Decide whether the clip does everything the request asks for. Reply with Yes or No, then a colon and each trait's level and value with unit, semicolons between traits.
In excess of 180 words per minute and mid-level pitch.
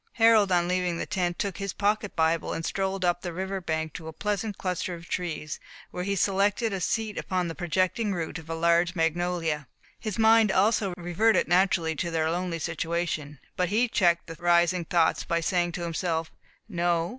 Yes: average, 190 wpm; medium, 175 Hz